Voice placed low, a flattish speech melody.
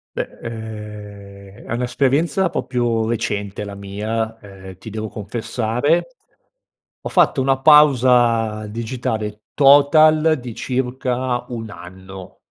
No: low, 115 Hz; average, 3.6 semitones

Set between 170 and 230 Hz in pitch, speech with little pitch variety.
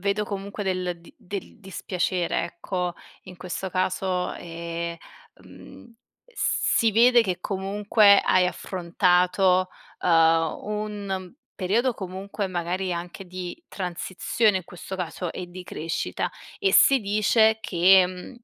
Yes: medium, 185 Hz; narrow, 2.1 semitones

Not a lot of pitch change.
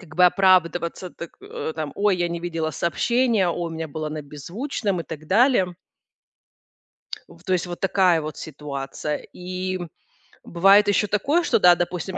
No: average, 3.2 semitones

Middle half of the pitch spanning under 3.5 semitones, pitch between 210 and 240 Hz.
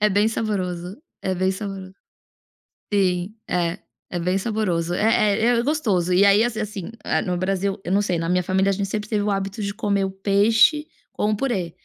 No: narrow, 2.5 semitones; high, 195 Hz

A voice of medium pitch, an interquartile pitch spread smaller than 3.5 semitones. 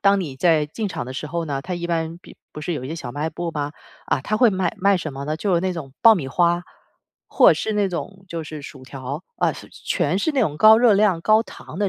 No: medium, 170 Hz; average, 4.9 semitones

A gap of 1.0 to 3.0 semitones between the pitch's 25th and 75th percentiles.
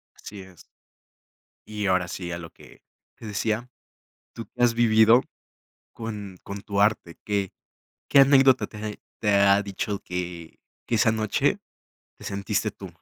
Yes: narrow, 2.4 semitones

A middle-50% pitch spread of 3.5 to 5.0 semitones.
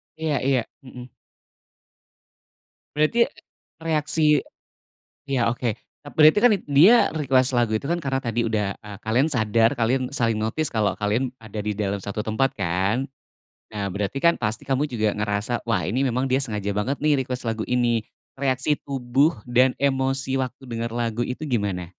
Yes: average, 4.0 semitones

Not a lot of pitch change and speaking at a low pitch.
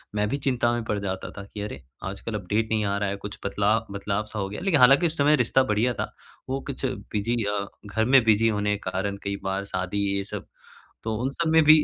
No: average, 4.1 semitones; low, 105 Hz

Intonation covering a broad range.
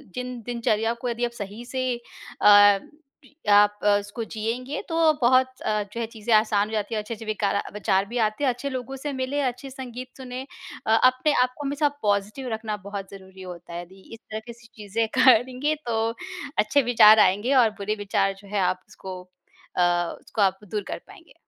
No: average, 3.7 semitones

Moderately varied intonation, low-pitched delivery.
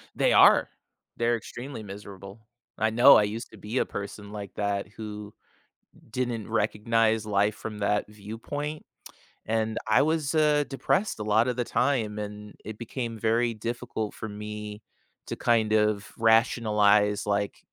No: narrow, 2.1 semitones; low, 110 Hz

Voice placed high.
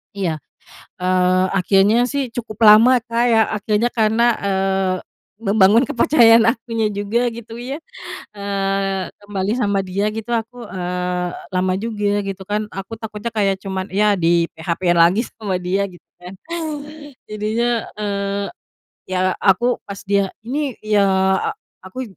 Yes: high, 205 Hz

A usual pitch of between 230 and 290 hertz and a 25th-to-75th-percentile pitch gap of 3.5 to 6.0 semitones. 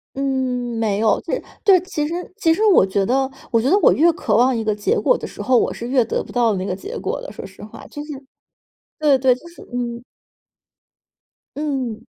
Yes: very high, 255 Hz; average, 5.1 semitones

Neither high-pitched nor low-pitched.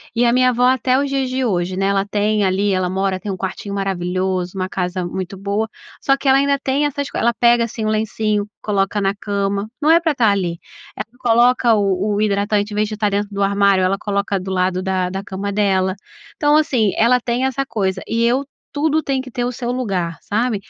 No: high, 205 Hz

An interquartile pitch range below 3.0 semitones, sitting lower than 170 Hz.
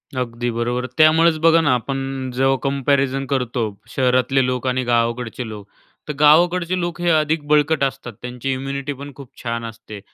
No: average, 3.3 semitones; low, 135 Hz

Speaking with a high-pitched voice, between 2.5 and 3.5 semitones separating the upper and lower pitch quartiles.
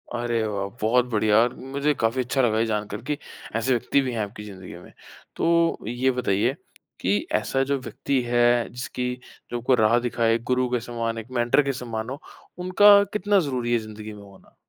No: low, 120 Hz; average, 3.0 semitones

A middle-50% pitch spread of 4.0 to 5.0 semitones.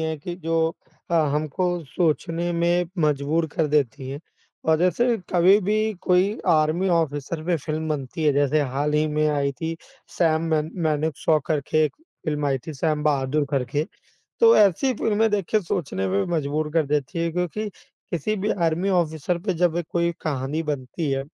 No: average, 2.9 semitones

